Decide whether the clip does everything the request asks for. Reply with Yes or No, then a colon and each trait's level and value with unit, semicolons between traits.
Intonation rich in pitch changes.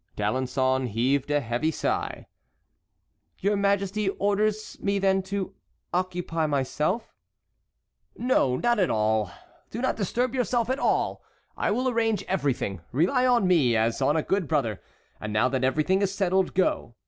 Yes: wide, 7.6 semitones